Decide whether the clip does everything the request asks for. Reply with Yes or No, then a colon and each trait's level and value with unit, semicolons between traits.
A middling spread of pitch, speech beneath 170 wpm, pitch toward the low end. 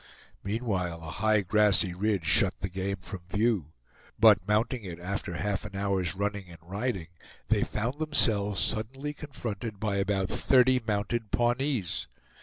Yes: average, 3.4 semitones; average, 145 wpm; low, 100 Hz